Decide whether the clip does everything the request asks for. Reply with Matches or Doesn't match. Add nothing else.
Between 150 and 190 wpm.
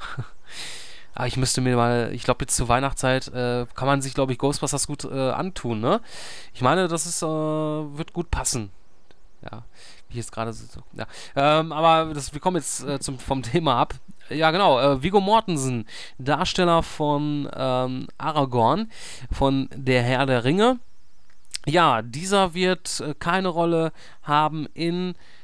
Matches